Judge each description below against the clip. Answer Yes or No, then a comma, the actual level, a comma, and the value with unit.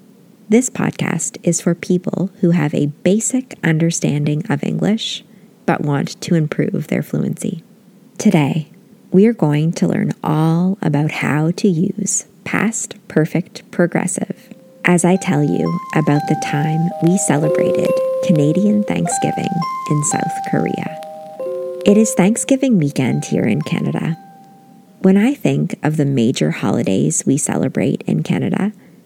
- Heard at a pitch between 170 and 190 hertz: Yes, medium, 185 Hz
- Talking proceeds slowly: Yes, slow, 130 wpm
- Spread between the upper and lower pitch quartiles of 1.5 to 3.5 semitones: No, average, 4.6 semitones